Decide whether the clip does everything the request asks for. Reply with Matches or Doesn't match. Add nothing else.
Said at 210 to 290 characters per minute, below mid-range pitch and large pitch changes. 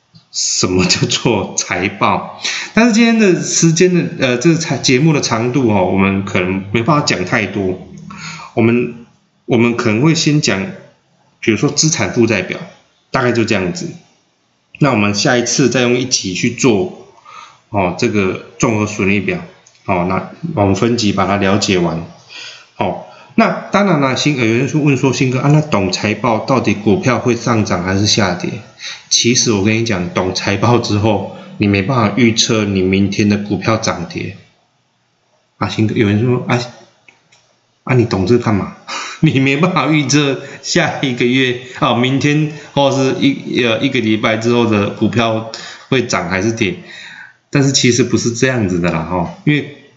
Doesn't match